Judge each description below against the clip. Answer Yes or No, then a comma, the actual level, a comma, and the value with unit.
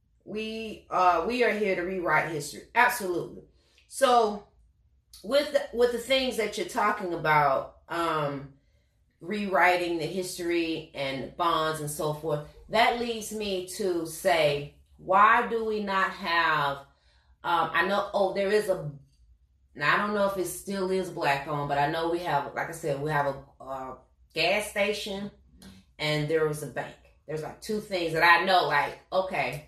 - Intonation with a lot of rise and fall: Yes, wide, 5.7 semitones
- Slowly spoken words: No, average, 170 wpm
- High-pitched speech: No, medium, 170 Hz